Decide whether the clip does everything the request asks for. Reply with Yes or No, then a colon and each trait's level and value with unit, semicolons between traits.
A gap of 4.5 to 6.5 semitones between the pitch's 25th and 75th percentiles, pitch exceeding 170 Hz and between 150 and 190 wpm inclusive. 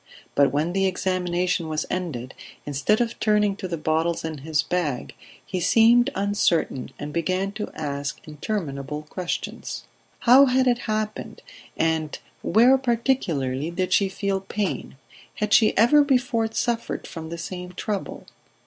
No: wide, 5.4 semitones; medium, 185 Hz; average, 140 wpm